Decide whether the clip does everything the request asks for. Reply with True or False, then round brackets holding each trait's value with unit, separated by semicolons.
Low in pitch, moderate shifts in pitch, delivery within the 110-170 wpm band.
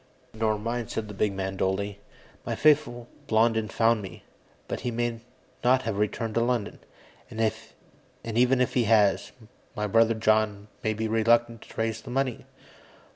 False (115 Hz; 1.9 semitones; 160 wpm)